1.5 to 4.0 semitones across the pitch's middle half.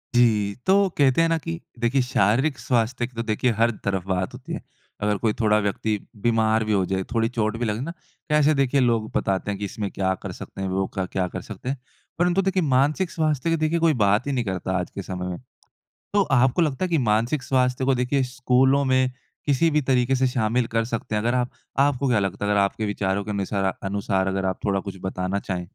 No: average, 4.9 semitones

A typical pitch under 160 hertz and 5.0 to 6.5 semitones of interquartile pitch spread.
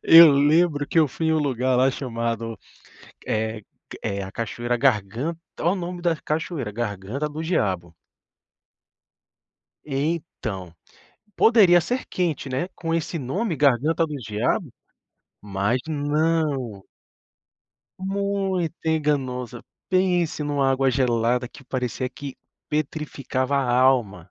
Yes: medium, 140 Hz; wide, 5.4 semitones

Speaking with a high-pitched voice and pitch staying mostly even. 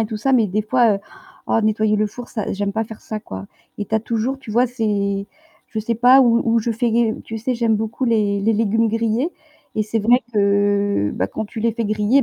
Yes: high, 220 Hz; narrow, 2.0 semitones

